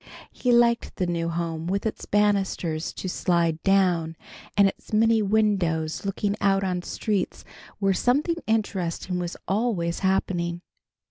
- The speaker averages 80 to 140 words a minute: Yes, slow, 135 wpm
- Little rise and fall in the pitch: No, average, 3.5 semitones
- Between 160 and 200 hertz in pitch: Yes, high, 190 Hz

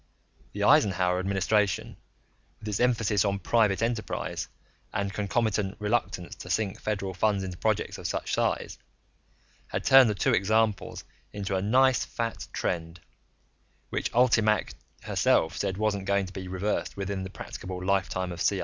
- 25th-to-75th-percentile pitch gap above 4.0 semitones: No, narrow, 2.4 semitones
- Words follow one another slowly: No, average, 150 wpm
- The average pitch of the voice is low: Yes, low, 100 Hz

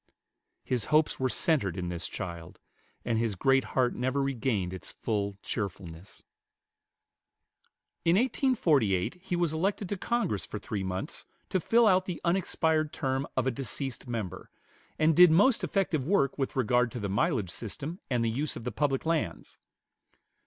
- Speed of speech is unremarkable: Yes, average, 160 wpm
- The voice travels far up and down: Yes, wide, 7.6 semitones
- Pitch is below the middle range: Yes, low, 130 Hz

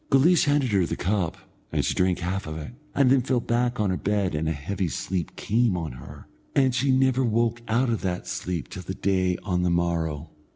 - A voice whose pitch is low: Yes, very low, 95 Hz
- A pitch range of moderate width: No, wide, 5.8 semitones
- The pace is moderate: No, fast, 220 wpm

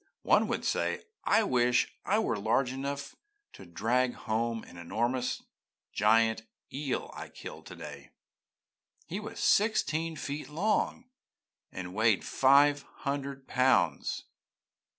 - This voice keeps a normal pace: No, slow, 115 wpm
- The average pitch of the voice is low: Yes, low, 130 Hz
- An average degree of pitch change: Yes, average, 4.3 semitones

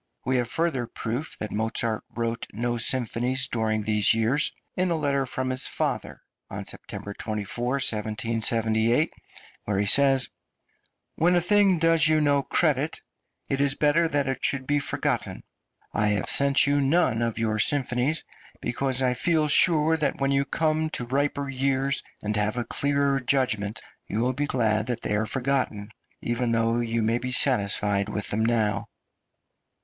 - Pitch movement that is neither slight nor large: Yes, average, 4.1 semitones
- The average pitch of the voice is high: No, low, 125 Hz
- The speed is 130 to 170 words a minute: Yes, average, 165 wpm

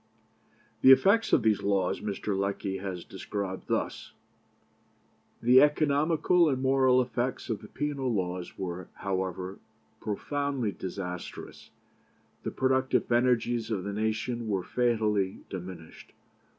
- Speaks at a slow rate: Yes, slow, 120 wpm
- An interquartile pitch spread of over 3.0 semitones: Yes, average, 5.3 semitones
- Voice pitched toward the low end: Yes, low, 110 Hz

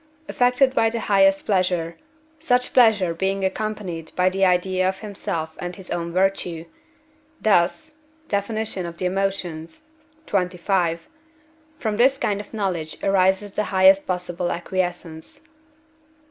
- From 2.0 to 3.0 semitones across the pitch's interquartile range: Yes, average, 2.7 semitones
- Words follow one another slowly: Yes, slow, 125 wpm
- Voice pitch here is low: No, high, 190 Hz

